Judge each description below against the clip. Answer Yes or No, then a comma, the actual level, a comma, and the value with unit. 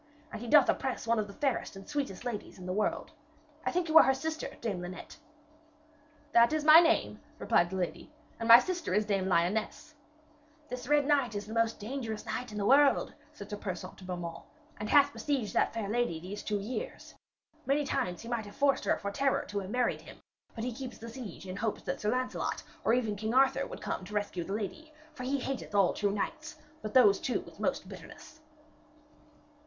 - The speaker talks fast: Yes, fast, 210 wpm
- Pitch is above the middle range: Yes, high, 230 Hz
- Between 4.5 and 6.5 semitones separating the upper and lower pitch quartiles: Yes, average, 5.1 semitones